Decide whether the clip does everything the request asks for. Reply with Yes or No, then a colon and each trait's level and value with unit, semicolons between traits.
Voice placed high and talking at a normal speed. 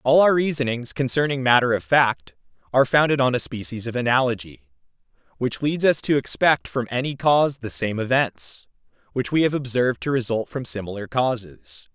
No: low, 125 Hz; average, 170 wpm